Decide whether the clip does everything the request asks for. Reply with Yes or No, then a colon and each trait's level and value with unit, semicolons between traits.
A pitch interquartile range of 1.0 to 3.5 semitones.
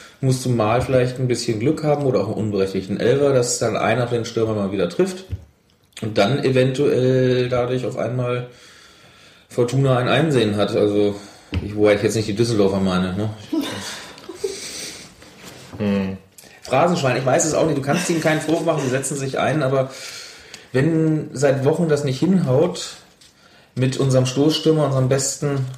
No: average, 4.8 semitones